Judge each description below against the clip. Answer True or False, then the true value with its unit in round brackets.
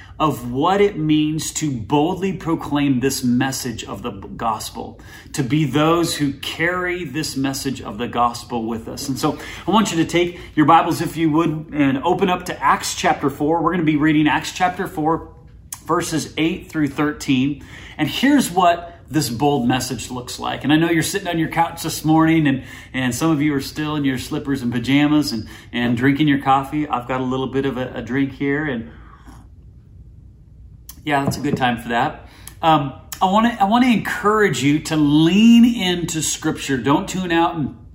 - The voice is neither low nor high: True (150 Hz)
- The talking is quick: False (195 wpm)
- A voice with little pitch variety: False (3.8 semitones)